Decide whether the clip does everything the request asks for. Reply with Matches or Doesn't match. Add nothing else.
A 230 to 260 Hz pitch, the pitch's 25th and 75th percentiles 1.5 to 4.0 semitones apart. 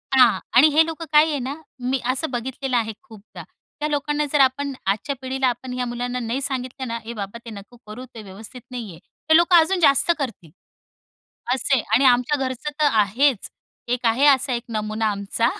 Matches